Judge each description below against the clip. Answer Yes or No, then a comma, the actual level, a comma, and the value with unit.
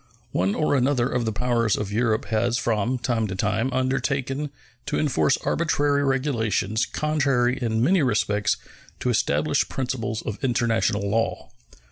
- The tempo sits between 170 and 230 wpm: No, average, 140 wpm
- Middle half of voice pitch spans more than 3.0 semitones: Yes, average, 3.4 semitones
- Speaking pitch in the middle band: No, low, 120 Hz